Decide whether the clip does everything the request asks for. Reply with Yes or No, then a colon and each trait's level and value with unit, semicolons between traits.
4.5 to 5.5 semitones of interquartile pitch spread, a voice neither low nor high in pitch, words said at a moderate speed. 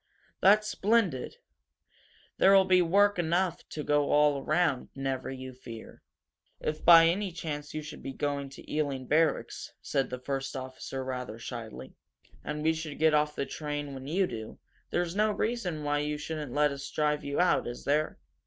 No: average, 3.7 semitones; medium, 150 Hz; average, 170 wpm